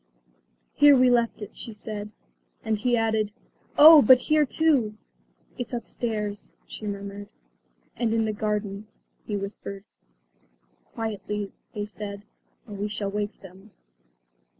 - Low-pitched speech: No, high, 215 Hz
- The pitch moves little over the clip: Yes, narrow, 2.3 semitones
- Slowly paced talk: Yes, slow, 125 wpm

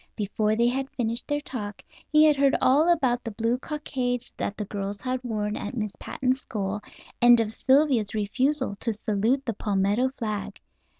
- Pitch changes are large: No, average, 3.9 semitones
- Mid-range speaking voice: No, high, 240 Hz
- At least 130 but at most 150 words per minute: No, average, 175 wpm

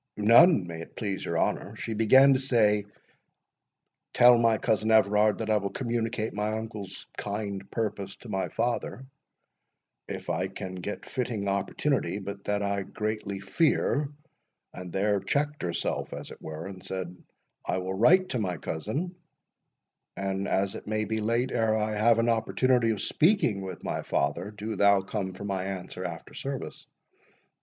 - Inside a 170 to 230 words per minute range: No, average, 155 wpm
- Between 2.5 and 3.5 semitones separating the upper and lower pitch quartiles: Yes, average, 3.1 semitones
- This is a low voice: Yes, low, 105 Hz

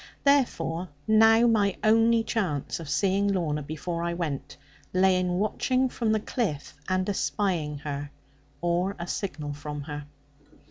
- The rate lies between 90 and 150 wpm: Yes, average, 140 wpm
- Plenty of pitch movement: Yes, wide, 6.1 semitones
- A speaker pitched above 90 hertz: Yes, medium, 185 Hz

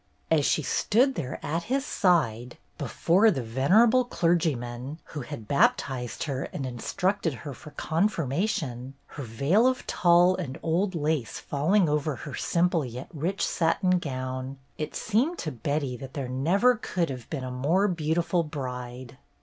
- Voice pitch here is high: No, medium, 155 Hz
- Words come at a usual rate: Yes, average, 155 wpm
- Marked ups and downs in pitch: Yes, wide, 5.7 semitones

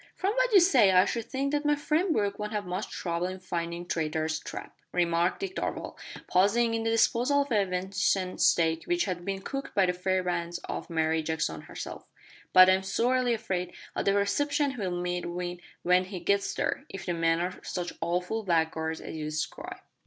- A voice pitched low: No, medium, 185 Hz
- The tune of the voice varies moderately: Yes, average, 4.7 semitones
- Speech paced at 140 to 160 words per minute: No, average, 195 wpm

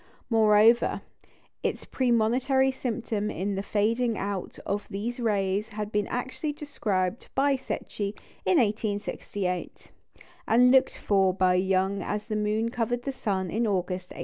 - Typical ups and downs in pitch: Yes, average, 3.5 semitones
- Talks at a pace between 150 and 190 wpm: No, average, 140 wpm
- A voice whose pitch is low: No, high, 210 Hz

